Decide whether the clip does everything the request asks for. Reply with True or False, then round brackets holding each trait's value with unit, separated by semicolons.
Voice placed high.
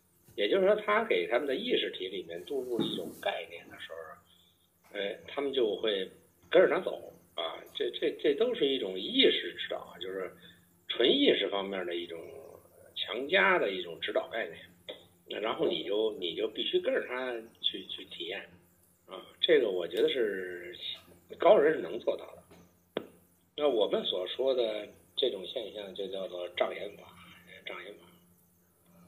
True (375 Hz)